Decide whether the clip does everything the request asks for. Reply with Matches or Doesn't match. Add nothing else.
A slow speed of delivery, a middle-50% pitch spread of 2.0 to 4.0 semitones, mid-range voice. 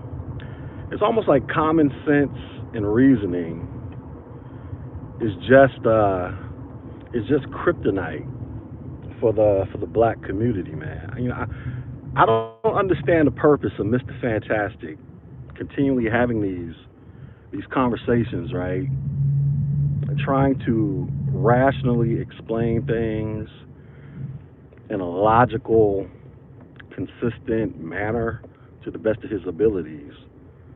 Doesn't match